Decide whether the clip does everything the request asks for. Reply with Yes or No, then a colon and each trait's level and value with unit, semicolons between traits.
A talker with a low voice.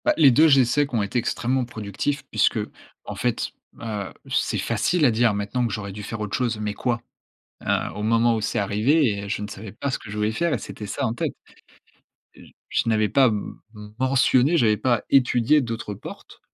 Yes: low, 115 Hz